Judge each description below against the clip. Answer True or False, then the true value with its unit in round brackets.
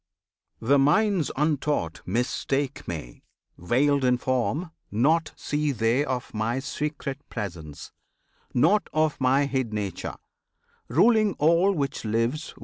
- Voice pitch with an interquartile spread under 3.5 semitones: False (4.6 semitones)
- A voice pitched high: False (135 Hz)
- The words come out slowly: True (115 wpm)